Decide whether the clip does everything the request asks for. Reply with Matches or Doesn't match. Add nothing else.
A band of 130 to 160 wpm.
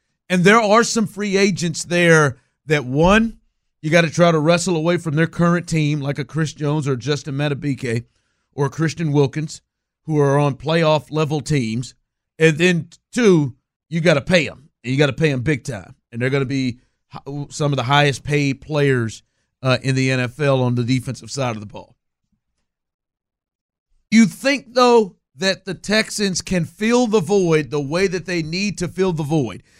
Doesn't match